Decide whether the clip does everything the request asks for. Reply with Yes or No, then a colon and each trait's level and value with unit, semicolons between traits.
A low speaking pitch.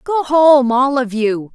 No: very high, 265 Hz